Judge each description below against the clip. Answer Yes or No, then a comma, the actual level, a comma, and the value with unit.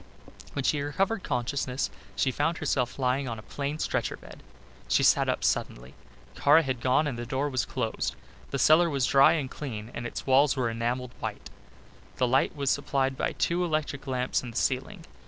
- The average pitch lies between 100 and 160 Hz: Yes, low, 135 Hz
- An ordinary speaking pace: Yes, average, 185 wpm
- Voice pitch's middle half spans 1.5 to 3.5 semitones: Yes, narrow, 2.6 semitones